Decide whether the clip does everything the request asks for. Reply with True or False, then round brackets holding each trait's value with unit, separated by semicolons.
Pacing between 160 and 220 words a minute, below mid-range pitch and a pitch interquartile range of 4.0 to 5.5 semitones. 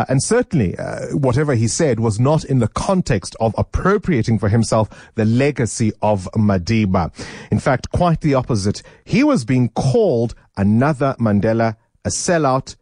False (150 wpm; 115 Hz; 4.7 semitones)